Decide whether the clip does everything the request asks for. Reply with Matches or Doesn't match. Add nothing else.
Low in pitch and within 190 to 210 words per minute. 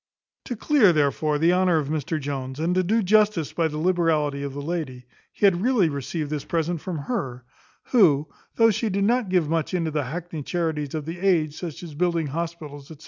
Doesn't match